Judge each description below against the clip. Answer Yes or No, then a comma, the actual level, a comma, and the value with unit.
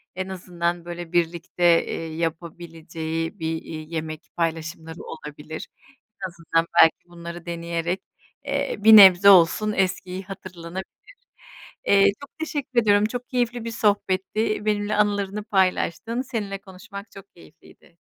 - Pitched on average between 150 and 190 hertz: Yes, medium, 185 Hz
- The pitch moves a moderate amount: Yes, average, 3.9 semitones